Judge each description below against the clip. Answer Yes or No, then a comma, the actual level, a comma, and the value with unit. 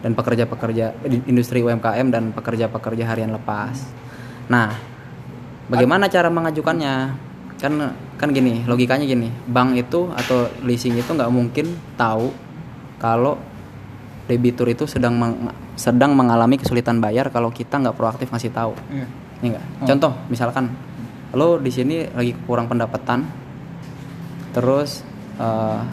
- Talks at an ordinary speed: Yes, average, 120 wpm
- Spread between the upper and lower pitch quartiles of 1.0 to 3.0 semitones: Yes, narrow, 2.6 semitones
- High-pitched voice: No, low, 125 Hz